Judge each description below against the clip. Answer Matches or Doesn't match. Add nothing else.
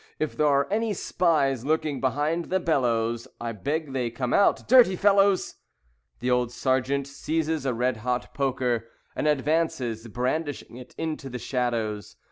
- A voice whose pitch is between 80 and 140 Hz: Matches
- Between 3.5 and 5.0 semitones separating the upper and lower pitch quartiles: Matches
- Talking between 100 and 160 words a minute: Matches